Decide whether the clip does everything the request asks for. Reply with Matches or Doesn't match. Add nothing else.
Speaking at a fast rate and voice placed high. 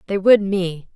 Doesn't match